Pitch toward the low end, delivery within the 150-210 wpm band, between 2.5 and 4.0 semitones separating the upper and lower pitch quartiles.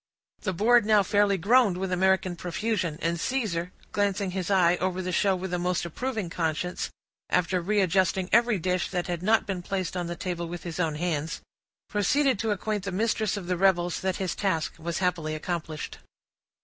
No: medium, 185 Hz; average, 185 wpm; average, 2.8 semitones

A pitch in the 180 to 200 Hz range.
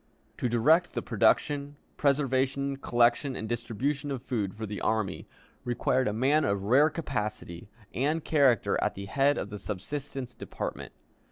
No: low, 125 Hz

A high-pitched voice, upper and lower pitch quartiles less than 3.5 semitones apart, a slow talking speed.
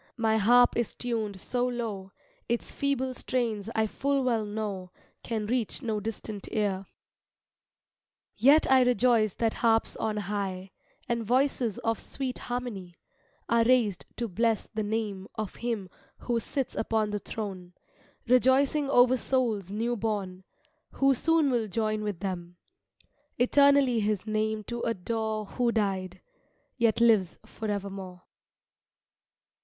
Yes: high, 220 Hz; average, 3.1 semitones; slow, 130 wpm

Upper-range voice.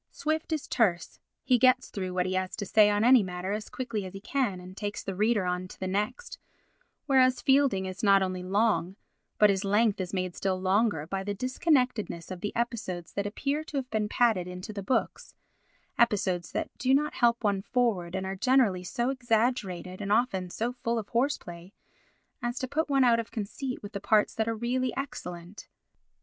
Yes: high, 210 Hz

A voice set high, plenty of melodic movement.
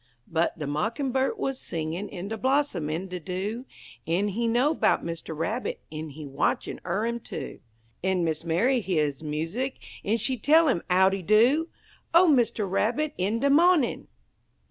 Yes: high, 205 Hz; wide, 7.5 semitones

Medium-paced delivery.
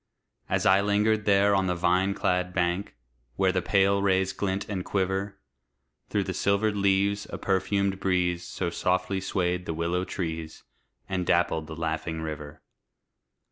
Yes: average, 150 wpm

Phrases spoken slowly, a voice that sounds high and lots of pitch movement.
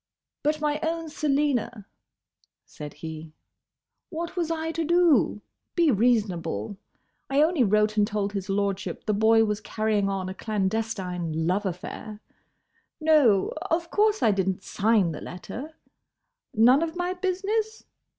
Yes: slow, 130 wpm; high, 220 Hz; wide, 8.3 semitones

